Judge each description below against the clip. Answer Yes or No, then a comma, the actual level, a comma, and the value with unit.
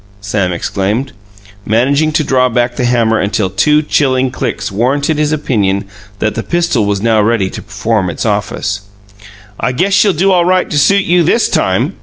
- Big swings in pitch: Yes, wide, 6.5 semitones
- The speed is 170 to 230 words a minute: Yes, average, 180 wpm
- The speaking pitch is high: No, low, 120 Hz